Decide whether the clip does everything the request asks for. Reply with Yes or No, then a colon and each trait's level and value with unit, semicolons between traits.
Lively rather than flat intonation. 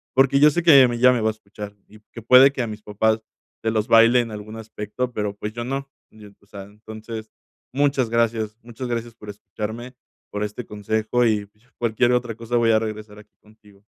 No: narrow, 2.4 semitones